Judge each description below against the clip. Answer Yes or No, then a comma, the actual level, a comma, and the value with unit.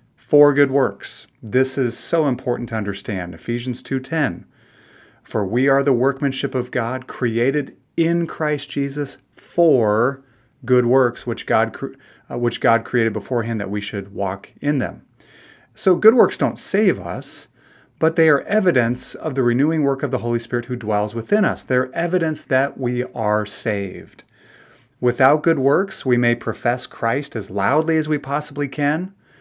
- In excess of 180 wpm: No, average, 165 wpm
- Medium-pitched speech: No, low, 130 Hz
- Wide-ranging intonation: No, average, 3.7 semitones